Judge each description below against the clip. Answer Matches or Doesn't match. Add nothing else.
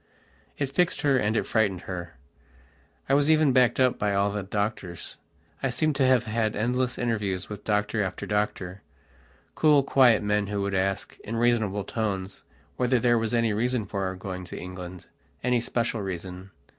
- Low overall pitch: Matches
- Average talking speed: Matches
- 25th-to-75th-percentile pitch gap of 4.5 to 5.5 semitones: Doesn't match